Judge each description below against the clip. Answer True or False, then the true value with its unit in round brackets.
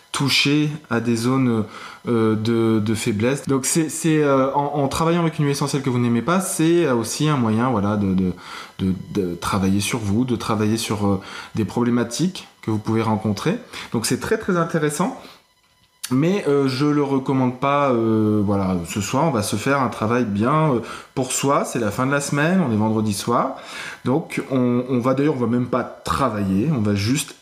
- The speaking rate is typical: True (205 wpm)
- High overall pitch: False (125 Hz)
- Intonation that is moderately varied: True (4.7 semitones)